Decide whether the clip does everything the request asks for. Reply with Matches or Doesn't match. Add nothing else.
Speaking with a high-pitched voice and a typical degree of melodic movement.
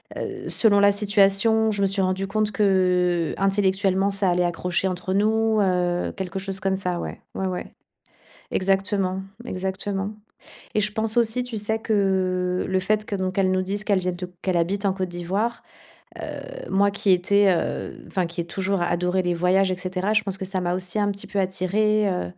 Doesn't match